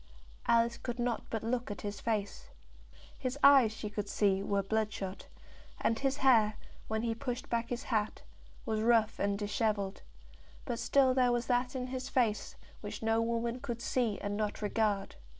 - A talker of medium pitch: No, high, 230 Hz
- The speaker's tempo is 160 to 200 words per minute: Yes, average, 170 wpm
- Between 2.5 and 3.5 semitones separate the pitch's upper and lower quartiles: Yes, average, 2.8 semitones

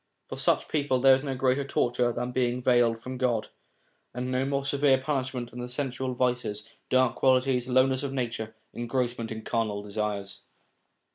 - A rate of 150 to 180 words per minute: Yes, average, 160 wpm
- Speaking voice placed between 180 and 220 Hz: No, low, 125 Hz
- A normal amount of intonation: No, narrow, 1.9 semitones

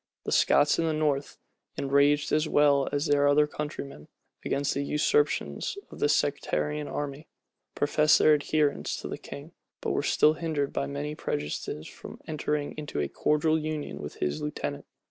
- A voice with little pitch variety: Yes, narrow, 1.2 semitones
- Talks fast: No, average, 165 wpm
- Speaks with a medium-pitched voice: Yes, medium, 145 Hz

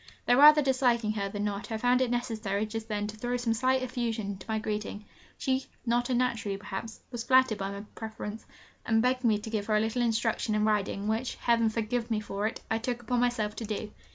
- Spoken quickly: Yes, fast, 220 wpm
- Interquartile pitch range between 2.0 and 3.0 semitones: Yes, narrow, 2.4 semitones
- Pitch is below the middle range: No, high, 225 Hz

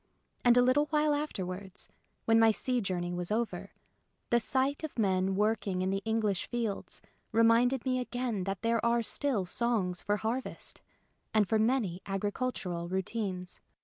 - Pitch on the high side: Yes, high, 220 Hz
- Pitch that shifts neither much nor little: Yes, average, 4.4 semitones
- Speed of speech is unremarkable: Yes, average, 150 wpm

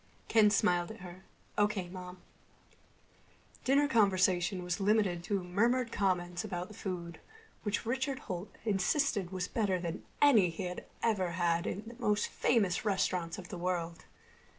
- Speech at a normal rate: Yes, average, 150 wpm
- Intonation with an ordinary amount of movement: Yes, average, 3.2 semitones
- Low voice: No, high, 190 Hz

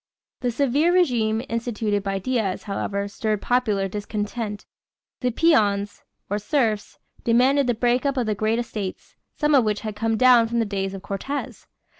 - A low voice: No, high, 225 Hz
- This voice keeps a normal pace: Yes, average, 165 wpm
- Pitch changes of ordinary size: Yes, average, 3.3 semitones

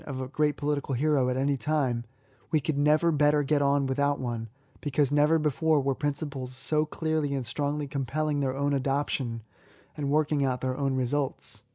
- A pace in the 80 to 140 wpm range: No, average, 185 wpm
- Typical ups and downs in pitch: No, narrow, 2.1 semitones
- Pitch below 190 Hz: Yes, medium, 140 Hz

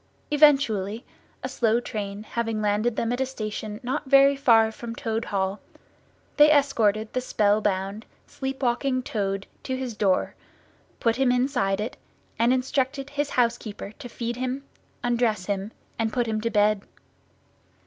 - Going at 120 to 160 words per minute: Yes, average, 150 wpm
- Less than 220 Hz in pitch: No, high, 230 Hz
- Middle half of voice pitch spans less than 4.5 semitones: Yes, average, 3.5 semitones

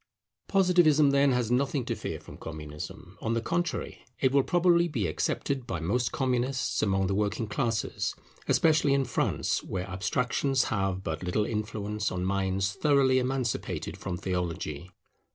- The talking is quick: No, average, 150 wpm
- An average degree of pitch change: No, wide, 6.1 semitones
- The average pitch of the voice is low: Yes, low, 115 Hz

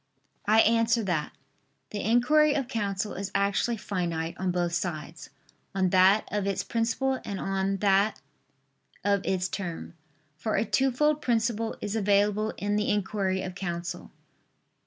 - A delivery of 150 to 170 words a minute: No, average, 140 wpm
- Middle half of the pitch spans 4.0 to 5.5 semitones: No, average, 3.2 semitones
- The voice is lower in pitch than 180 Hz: No, high, 200 Hz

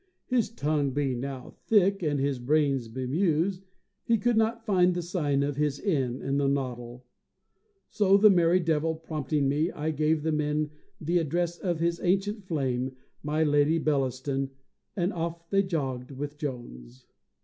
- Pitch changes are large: No, average, 4.3 semitones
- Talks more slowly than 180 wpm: Yes, average, 160 wpm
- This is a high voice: No, medium, 150 Hz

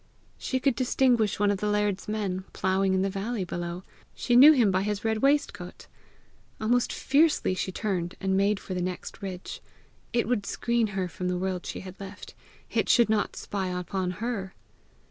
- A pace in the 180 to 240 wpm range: Yes, average, 185 wpm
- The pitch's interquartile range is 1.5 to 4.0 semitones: Yes, average, 3.4 semitones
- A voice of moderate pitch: No, high, 200 Hz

